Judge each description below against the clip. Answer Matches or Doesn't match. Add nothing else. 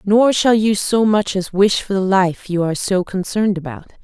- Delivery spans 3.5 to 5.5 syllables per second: Matches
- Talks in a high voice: Matches